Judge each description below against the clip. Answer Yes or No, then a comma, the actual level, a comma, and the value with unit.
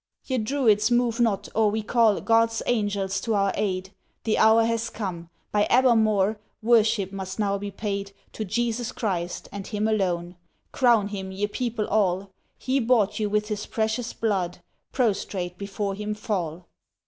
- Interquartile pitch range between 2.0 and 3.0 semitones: Yes, narrow, 2.5 semitones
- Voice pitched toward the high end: Yes, high, 210 Hz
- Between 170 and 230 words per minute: No, average, 160 wpm